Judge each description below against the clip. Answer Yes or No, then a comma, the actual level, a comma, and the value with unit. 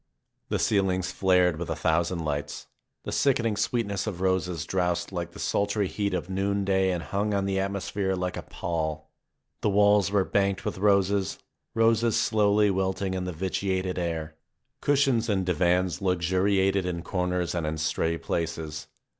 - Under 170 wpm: Yes, average, 155 wpm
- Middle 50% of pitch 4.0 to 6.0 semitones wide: No, narrow, 2.5 semitones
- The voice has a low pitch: Yes, very low, 95 Hz